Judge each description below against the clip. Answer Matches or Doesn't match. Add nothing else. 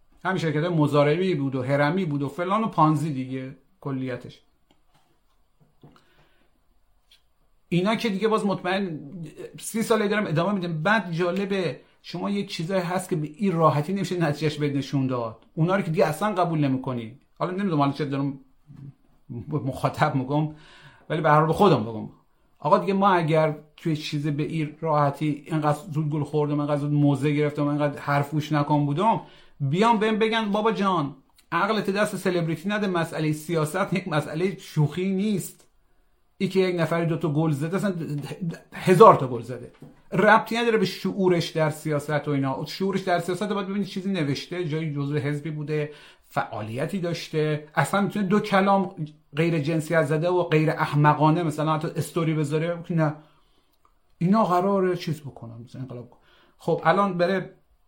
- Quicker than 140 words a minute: Matches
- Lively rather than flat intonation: Doesn't match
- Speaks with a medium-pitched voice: Matches